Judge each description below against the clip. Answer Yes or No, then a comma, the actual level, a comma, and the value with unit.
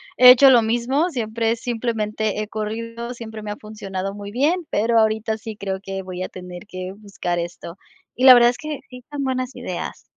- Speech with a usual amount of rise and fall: Yes, average, 3.2 semitones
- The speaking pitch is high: Yes, high, 220 Hz